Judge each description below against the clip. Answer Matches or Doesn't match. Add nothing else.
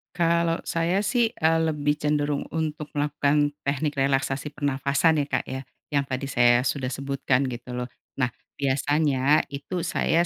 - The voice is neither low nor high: Matches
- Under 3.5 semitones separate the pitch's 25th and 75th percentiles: Matches